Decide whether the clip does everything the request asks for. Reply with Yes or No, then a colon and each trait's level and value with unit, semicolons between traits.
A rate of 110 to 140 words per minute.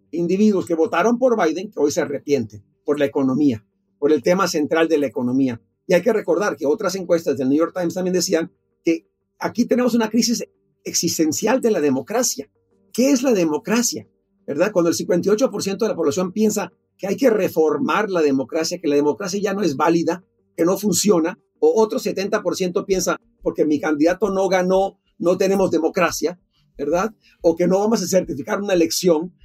No: average, 185 wpm